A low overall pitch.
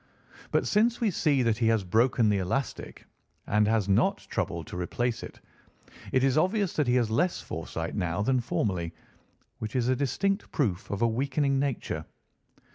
Yes: low, 120 Hz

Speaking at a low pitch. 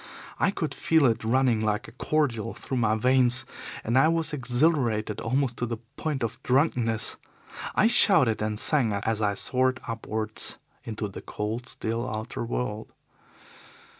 Yes: low, 120 Hz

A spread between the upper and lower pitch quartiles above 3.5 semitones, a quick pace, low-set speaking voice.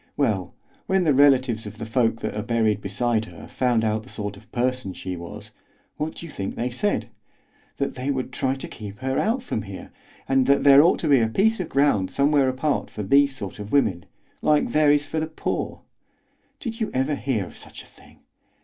Yes: average, 4.9 semitones; fast, 215 wpm; low, 130 Hz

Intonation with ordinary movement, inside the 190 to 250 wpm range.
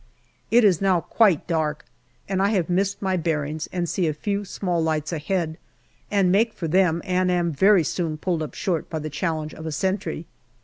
Yes: average, 3.3 semitones; average, 195 wpm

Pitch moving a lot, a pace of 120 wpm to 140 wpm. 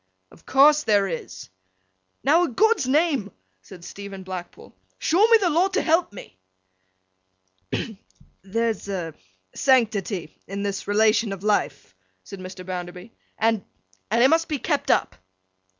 Yes: wide, 7.4 semitones; slow, 135 wpm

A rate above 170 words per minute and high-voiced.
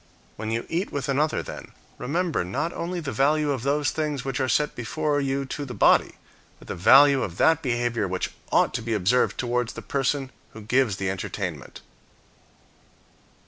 No: average, 180 wpm; low, 135 Hz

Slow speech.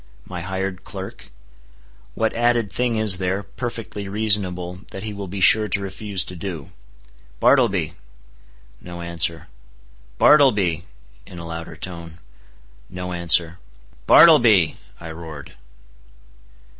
Yes: slow, 115 wpm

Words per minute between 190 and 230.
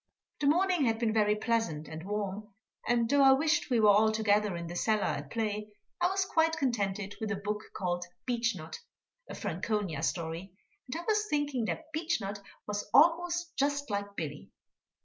No: average, 175 wpm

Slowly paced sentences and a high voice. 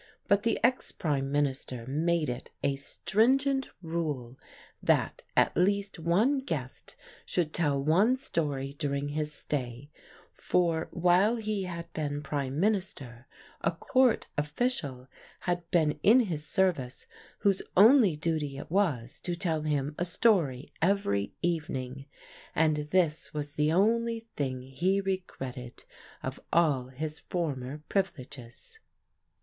No: slow, 125 wpm; medium, 160 Hz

